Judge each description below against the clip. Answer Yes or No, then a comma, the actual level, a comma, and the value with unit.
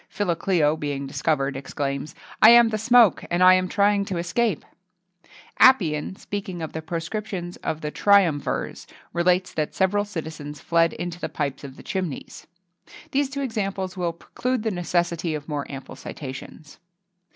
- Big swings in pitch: No, average, 4.9 semitones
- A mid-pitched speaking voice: Yes, medium, 175 Hz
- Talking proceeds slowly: No, average, 160 wpm